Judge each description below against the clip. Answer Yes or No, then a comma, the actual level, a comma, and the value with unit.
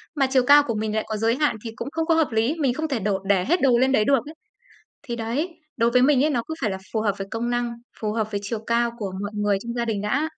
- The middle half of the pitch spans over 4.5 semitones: No, average, 4.2 semitones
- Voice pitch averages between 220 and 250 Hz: Yes, high, 235 Hz